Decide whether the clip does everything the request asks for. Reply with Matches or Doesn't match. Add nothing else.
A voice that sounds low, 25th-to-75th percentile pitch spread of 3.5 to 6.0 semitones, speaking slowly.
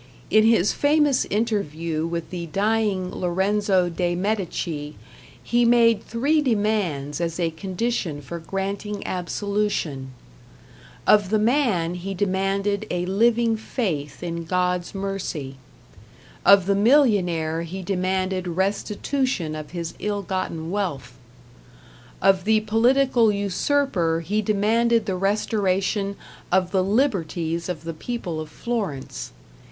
Doesn't match